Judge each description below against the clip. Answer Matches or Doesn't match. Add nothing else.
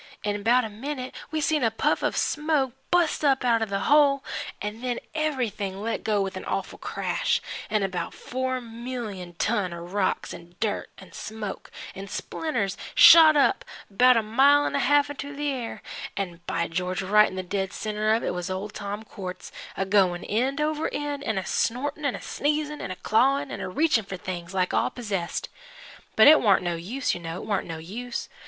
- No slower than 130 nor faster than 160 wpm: Doesn't match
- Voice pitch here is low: Doesn't match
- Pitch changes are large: Matches